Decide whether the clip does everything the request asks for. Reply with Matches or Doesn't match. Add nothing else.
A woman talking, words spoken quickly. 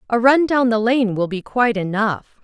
Matches